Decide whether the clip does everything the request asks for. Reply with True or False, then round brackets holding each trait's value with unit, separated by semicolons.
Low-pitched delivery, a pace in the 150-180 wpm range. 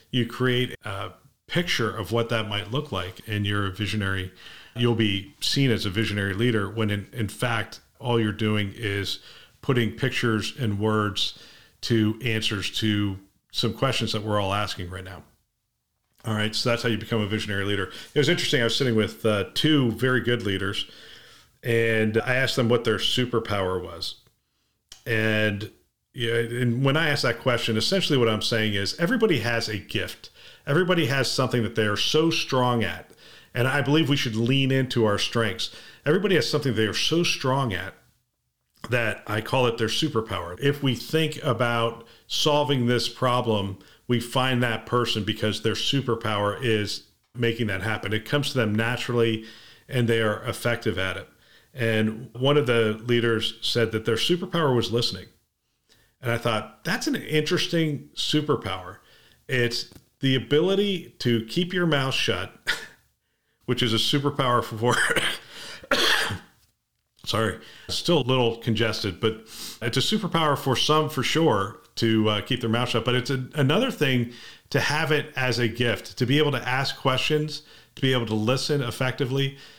True (115 Hz; 170 wpm)